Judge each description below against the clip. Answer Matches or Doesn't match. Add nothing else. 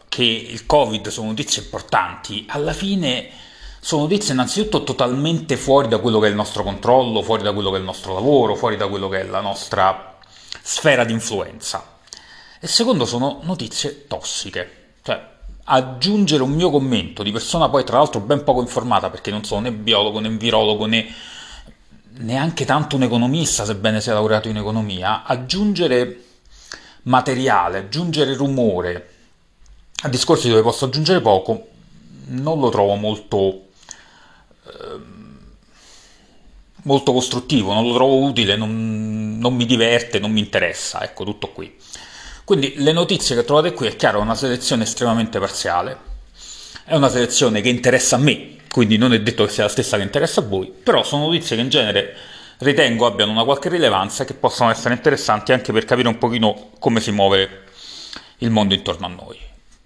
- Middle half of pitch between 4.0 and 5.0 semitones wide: Matches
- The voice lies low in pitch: Matches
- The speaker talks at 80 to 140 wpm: Doesn't match